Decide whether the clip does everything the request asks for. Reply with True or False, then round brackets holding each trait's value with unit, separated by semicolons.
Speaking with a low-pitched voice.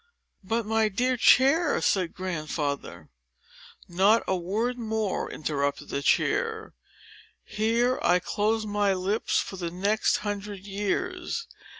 False (205 Hz)